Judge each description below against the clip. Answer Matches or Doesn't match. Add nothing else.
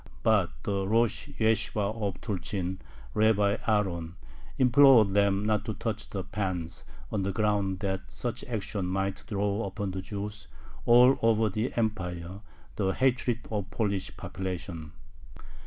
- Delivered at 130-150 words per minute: Matches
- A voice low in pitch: Matches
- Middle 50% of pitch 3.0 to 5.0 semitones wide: Doesn't match